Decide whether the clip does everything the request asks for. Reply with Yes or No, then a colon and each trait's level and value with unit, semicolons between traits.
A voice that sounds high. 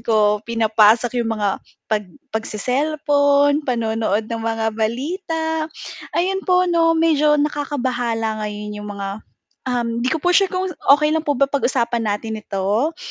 Yes: high, 245 Hz